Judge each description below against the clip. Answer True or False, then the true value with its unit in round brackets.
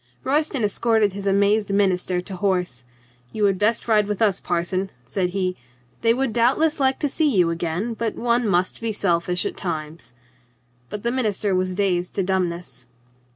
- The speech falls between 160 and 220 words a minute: True (170 wpm)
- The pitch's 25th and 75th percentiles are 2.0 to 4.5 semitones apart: True (4.0 semitones)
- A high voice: True (200 Hz)